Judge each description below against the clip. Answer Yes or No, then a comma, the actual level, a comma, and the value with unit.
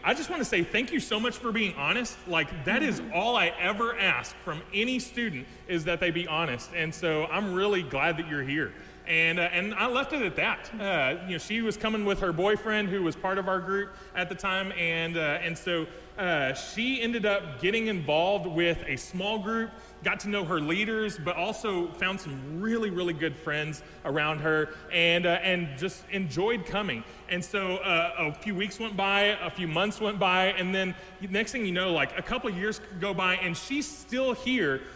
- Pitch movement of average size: Yes, average, 3.9 semitones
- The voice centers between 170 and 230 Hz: Yes, medium, 185 Hz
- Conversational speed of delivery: No, fast, 215 wpm